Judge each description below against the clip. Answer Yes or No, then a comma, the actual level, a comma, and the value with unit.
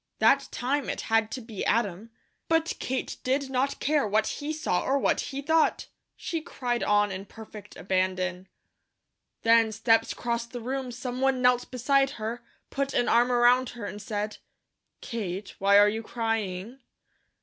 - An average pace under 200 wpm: Yes, average, 160 wpm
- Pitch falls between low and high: No, high, 235 Hz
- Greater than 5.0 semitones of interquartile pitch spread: No, average, 3.9 semitones